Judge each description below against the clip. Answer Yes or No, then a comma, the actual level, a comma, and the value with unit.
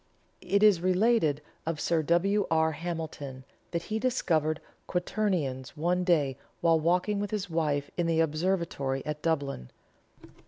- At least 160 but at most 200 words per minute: No, slow, 135 wpm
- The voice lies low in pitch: No, medium, 165 Hz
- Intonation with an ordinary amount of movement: Yes, average, 3.4 semitones